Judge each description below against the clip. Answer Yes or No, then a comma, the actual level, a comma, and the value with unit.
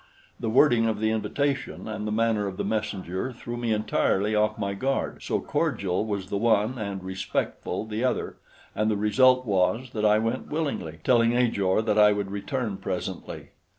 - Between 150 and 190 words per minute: Yes, average, 180 wpm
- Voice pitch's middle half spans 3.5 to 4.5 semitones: No, average, 2.7 semitones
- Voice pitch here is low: Yes, low, 110 Hz